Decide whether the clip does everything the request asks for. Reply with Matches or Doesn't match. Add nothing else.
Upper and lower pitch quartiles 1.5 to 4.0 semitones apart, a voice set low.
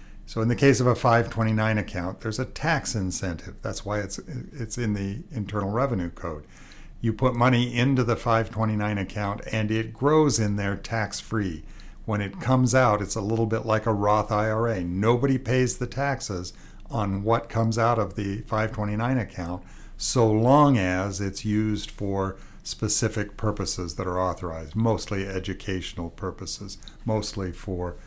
Matches